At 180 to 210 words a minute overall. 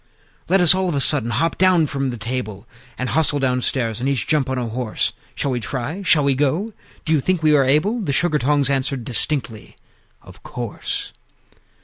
Yes: average, 200 wpm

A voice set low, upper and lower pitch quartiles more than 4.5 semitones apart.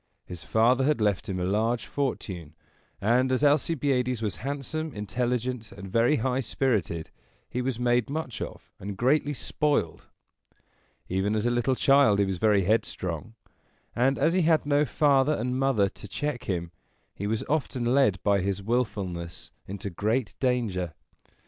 Yes: low, 120 Hz; average, 5.1 semitones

